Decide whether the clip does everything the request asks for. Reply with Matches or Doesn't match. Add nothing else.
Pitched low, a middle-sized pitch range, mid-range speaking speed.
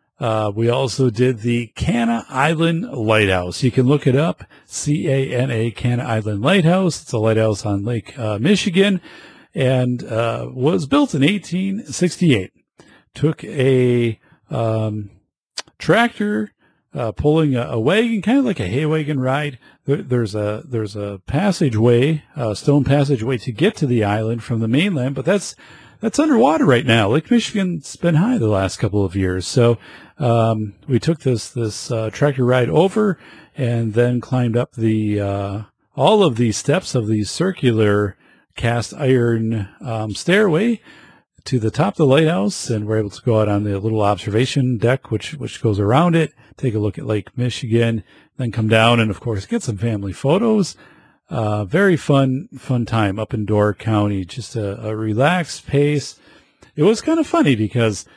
Doesn't match